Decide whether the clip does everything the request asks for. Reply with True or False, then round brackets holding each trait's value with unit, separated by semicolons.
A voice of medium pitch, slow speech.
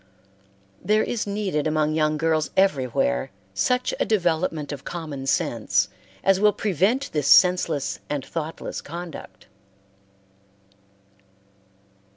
True (160 Hz; 105 wpm)